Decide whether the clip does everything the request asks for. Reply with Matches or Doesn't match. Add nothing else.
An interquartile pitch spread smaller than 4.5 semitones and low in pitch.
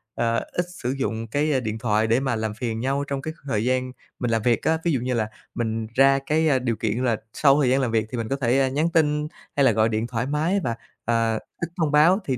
Matches